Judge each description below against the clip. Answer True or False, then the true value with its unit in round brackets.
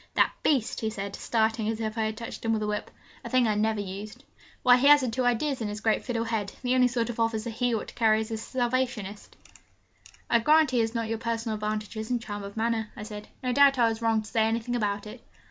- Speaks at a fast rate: True (250 wpm)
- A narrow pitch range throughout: True (2.1 semitones)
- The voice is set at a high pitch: True (225 Hz)